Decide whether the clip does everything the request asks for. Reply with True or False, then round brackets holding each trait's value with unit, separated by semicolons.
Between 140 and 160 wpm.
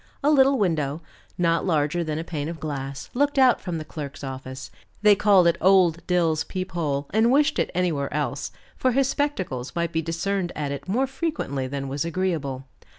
False (190 wpm)